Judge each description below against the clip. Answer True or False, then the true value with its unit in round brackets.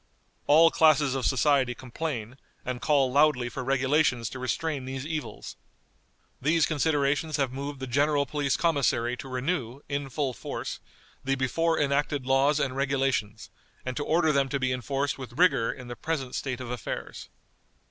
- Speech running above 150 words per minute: True (160 wpm)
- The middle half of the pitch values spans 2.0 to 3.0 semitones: True (2.5 semitones)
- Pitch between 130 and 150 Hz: True (135 Hz)